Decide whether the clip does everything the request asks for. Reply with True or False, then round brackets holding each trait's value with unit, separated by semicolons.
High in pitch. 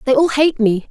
True (265 Hz)